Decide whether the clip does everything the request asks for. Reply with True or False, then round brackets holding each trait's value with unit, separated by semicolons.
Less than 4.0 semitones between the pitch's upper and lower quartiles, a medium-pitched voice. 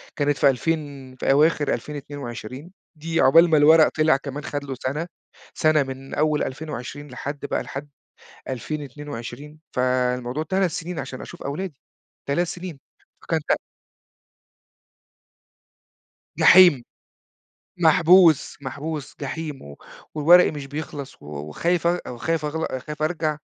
True (3.1 semitones; 150 Hz)